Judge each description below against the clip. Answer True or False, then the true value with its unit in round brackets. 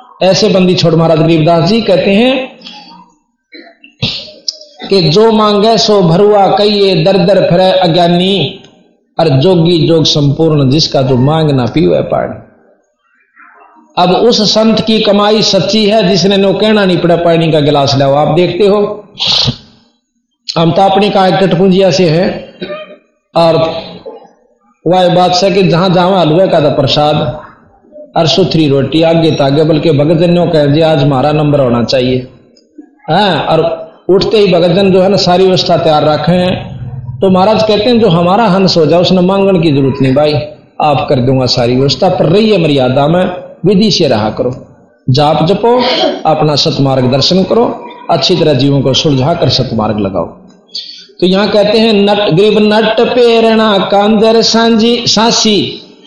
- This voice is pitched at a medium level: True (180 Hz)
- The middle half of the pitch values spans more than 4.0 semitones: True (5.0 semitones)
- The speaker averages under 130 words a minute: False (150 wpm)